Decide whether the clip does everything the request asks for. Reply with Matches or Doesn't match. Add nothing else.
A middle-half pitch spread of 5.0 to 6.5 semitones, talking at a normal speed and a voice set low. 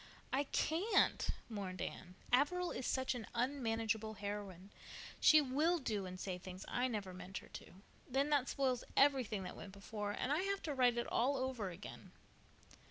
Doesn't match